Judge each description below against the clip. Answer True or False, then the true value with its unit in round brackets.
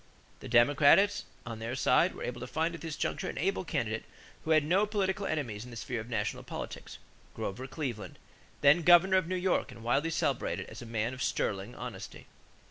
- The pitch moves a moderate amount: False (6.8 semitones)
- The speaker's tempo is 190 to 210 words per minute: True (200 wpm)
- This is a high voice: False (145 Hz)